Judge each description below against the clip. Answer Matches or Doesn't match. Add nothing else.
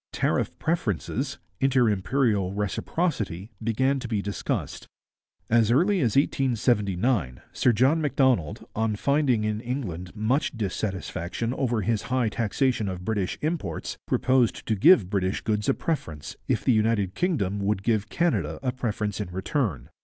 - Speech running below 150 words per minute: Matches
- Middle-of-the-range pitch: Doesn't match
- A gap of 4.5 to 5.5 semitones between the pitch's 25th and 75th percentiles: Matches